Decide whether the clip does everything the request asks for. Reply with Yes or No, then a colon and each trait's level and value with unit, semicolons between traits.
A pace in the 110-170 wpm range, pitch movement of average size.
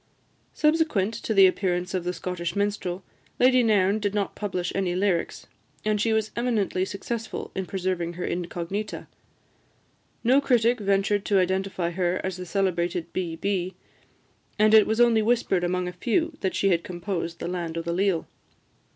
Yes: average, 165 wpm; average, 3.2 semitones